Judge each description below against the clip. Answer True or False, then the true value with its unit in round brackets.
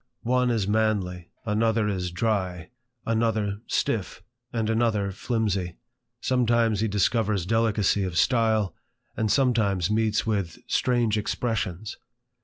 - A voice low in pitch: True (110 Hz)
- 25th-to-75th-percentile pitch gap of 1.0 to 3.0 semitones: True (2.5 semitones)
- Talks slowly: True (110 wpm)